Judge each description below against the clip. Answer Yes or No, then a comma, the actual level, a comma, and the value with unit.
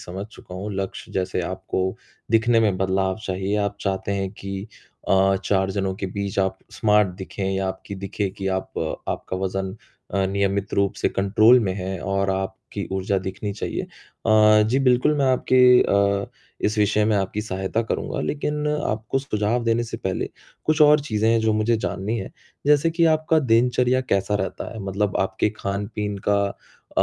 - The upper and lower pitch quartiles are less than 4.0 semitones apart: Yes, average, 2.8 semitones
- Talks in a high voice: No, low, 100 Hz